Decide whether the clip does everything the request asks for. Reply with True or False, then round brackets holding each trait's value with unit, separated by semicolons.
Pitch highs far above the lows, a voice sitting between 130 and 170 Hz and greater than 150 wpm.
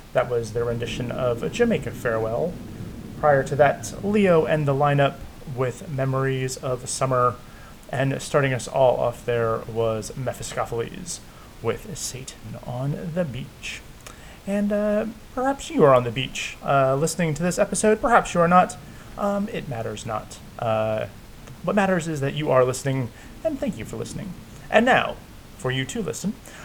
True (7.0 semitones; 135 Hz; 160 wpm)